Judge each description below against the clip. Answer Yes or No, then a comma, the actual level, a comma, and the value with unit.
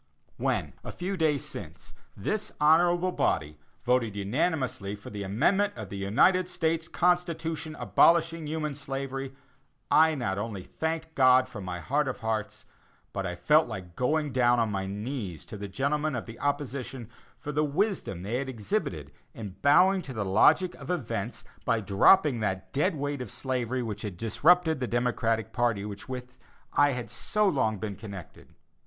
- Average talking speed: Yes, average, 165 wpm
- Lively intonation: Yes, wide, 6.7 semitones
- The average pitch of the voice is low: Yes, low, 130 Hz